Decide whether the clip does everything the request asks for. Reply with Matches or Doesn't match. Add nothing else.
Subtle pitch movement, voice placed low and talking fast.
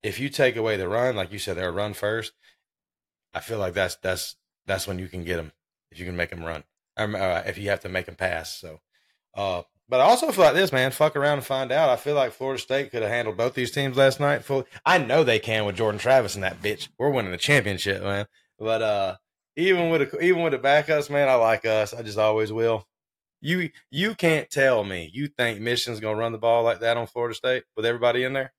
Doesn't match